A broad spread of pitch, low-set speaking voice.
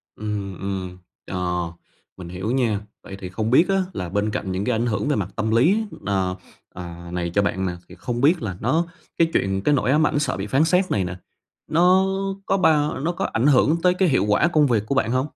Yes: wide, 7.8 semitones; low, 115 Hz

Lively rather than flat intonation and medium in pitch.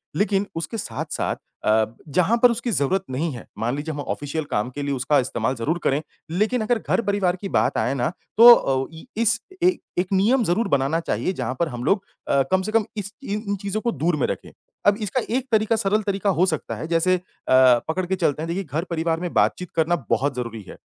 Yes: wide, 6.4 semitones; medium, 175 Hz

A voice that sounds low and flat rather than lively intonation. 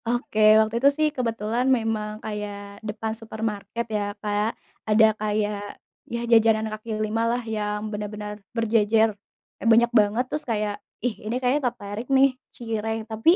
No: high, 220 Hz; narrow, 1.6 semitones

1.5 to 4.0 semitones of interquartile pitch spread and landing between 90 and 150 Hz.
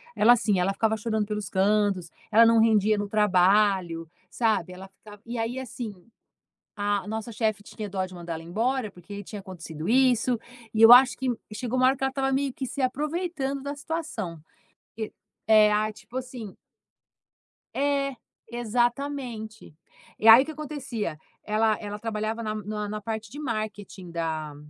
No: average, 3.7 semitones; high, 220 Hz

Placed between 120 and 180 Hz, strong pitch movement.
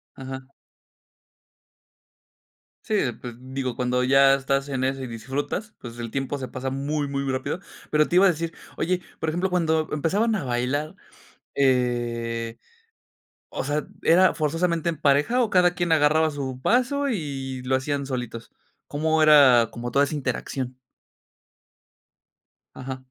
No: medium, 140 Hz; average, 3.7 semitones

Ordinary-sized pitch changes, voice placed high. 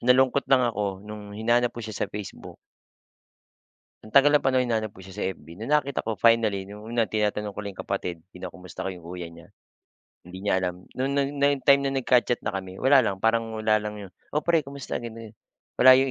No: average, 4.6 semitones; low, 110 Hz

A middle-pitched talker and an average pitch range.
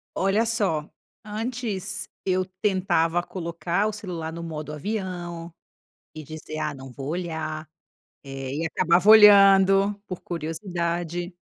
Yes: medium, 175 Hz; average, 3.5 semitones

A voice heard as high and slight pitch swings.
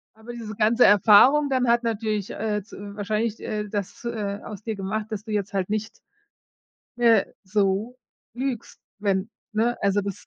Yes: high, 215 Hz; narrow, 2.3 semitones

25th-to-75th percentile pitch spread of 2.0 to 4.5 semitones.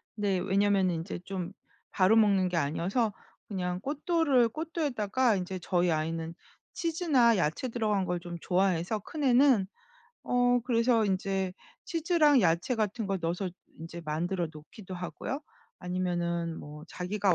No: wide, 5.4 semitones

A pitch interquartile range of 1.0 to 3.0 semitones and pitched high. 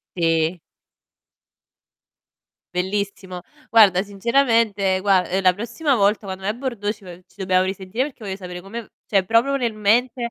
No: average, 3.6 semitones; high, 200 Hz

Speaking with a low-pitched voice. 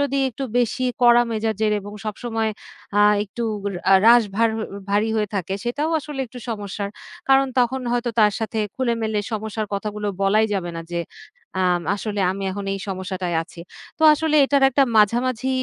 No: high, 220 Hz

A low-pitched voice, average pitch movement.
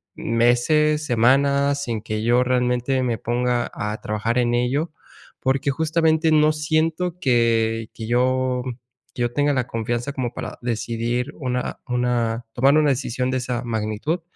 Yes: low, 125 Hz; average, 3.1 semitones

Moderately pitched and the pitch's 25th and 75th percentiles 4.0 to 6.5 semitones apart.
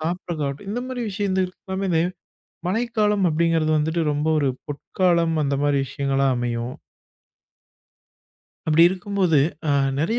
Yes: medium, 165 Hz; average, 4.7 semitones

